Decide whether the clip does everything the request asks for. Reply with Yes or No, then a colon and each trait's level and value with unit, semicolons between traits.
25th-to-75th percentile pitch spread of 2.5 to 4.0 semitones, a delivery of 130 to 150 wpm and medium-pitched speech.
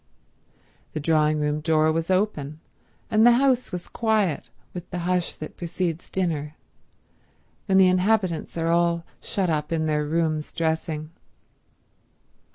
Yes: average, 3.1 semitones; slow, 135 wpm; medium, 165 Hz